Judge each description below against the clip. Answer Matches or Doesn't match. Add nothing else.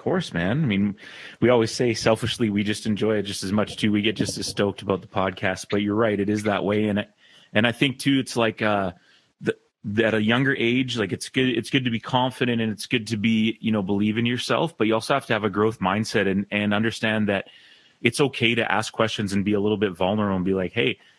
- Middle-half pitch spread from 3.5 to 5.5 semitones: Doesn't match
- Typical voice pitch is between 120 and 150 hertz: Doesn't match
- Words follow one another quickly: Matches